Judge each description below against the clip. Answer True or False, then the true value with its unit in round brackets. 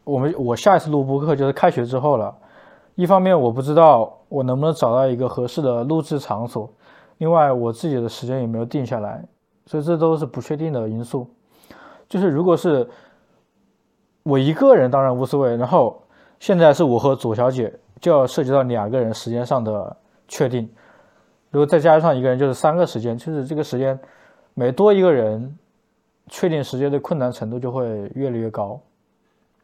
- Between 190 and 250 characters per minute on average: False (285 characters per minute)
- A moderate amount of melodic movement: True (4.2 semitones)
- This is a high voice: False (135 Hz)